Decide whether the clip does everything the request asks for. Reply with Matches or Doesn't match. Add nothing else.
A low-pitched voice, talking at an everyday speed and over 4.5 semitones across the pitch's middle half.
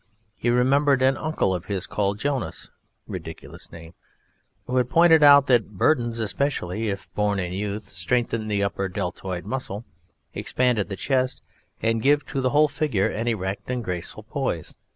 Matches